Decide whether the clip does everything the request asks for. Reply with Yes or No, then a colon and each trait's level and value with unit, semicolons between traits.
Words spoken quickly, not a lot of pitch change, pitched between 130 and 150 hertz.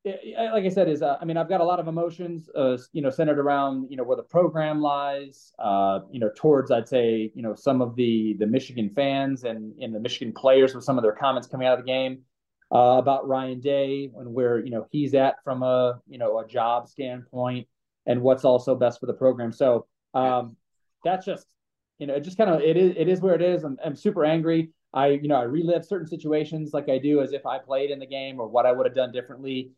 No: fast, 245 wpm; average, 3.7 semitones; low, 135 Hz